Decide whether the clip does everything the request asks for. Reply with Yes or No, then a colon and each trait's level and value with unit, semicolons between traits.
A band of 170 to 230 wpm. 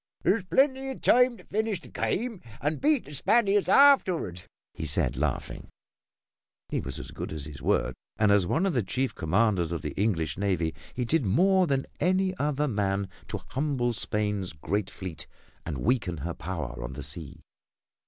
Yes: average, 175 wpm